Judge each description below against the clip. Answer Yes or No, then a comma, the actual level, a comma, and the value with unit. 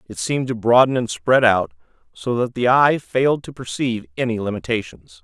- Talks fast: No, average, 185 wpm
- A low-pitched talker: Yes, low, 115 Hz